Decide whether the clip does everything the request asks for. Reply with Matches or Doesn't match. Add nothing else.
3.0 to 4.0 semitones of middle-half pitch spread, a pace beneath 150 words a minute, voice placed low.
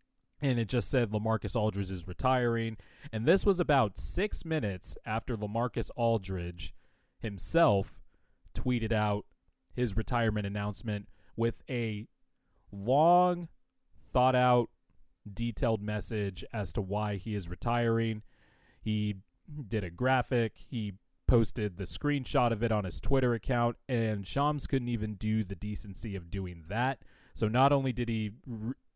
Matches